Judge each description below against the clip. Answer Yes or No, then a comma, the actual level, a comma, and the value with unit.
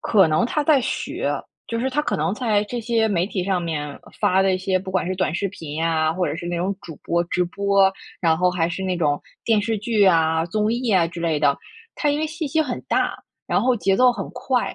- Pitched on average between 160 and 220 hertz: Yes, high, 190 Hz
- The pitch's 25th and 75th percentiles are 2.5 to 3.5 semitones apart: No, average, 5.3 semitones